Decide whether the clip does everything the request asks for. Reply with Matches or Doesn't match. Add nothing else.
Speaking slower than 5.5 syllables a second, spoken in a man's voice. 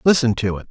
Doesn't match